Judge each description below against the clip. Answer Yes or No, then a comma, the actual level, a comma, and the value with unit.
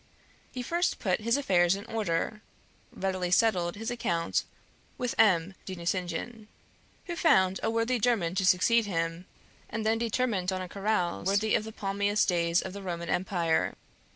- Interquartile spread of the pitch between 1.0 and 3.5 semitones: No, average, 4.0 semitones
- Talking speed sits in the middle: Yes, average, 160 wpm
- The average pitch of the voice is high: Yes, high, 195 Hz